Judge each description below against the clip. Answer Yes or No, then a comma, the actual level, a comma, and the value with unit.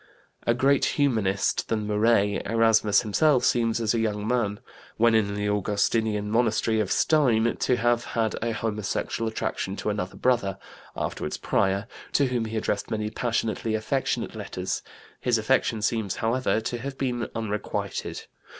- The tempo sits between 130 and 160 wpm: Yes, average, 150 wpm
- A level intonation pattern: Yes, narrow, 2.3 semitones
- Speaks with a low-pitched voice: Yes, low, 110 Hz